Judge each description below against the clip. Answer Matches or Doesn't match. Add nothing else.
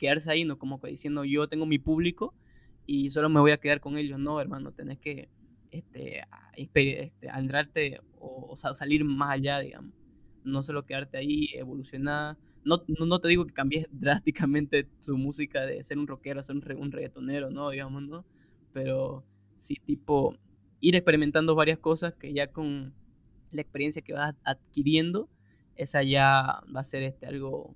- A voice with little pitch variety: Matches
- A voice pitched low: Doesn't match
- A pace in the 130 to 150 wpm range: Doesn't match